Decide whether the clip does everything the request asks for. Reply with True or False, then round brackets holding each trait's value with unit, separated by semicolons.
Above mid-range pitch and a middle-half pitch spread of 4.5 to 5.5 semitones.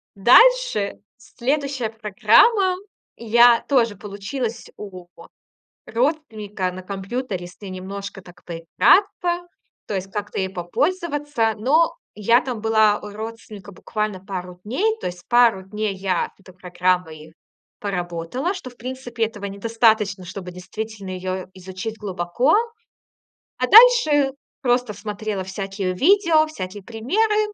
True (215 Hz; 5.1 semitones)